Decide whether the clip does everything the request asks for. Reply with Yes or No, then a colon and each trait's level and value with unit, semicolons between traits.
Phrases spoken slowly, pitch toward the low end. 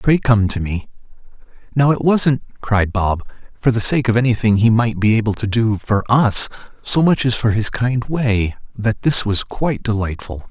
No: average, 195 wpm; low, 115 Hz